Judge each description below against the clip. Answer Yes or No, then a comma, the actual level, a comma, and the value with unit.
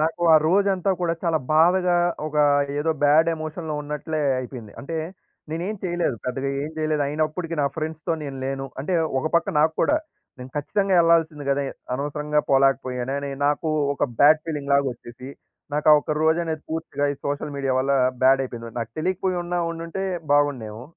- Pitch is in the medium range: Yes, medium, 150 Hz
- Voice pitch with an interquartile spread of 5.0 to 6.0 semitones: No, average, 3.3 semitones